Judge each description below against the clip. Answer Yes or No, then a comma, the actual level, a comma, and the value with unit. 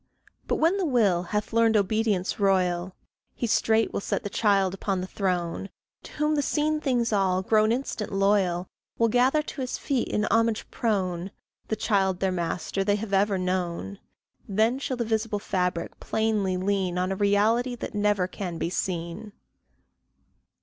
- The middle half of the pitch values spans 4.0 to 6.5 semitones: No, average, 3.4 semitones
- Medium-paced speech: Yes, average, 165 wpm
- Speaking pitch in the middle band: No, high, 205 Hz